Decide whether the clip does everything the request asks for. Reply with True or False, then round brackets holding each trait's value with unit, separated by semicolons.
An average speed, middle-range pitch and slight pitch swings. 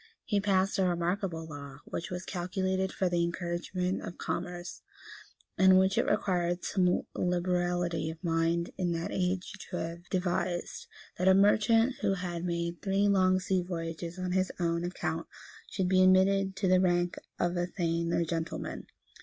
True (160 wpm; 180 Hz; 1.7 semitones)